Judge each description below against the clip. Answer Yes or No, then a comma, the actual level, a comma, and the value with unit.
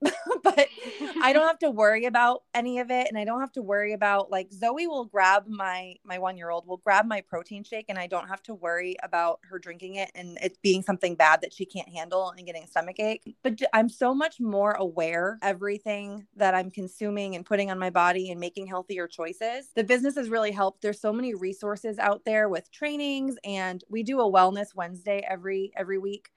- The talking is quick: Yes, fast, 220 wpm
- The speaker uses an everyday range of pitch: Yes, average, 3.3 semitones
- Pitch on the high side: Yes, high, 200 Hz